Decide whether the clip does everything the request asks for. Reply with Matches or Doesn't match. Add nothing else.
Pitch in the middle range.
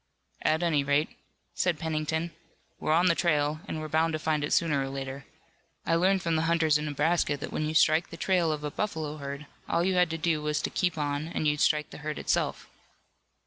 Matches